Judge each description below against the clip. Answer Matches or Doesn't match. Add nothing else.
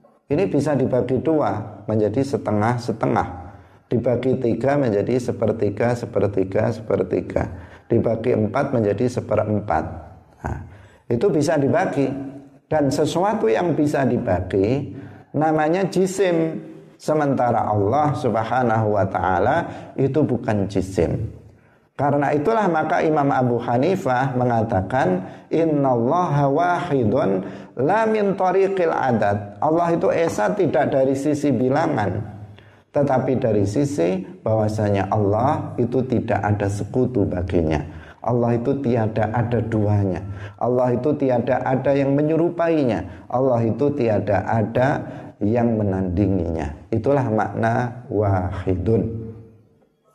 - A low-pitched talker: Matches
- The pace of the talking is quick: Doesn't match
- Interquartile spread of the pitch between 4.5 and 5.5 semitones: Matches